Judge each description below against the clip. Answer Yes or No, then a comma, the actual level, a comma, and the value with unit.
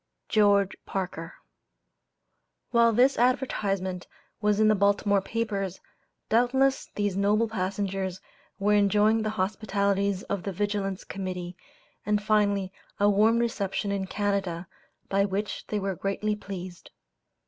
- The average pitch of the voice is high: Yes, high, 200 Hz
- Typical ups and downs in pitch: No, narrow, 1.7 semitones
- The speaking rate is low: Yes, slow, 120 wpm